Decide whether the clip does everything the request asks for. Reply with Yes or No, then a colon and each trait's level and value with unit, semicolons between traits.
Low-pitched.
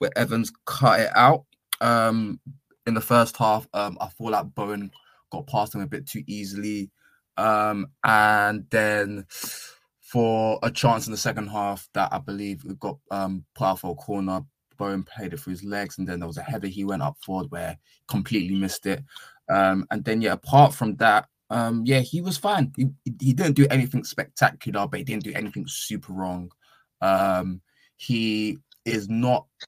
Yes: low, 105 Hz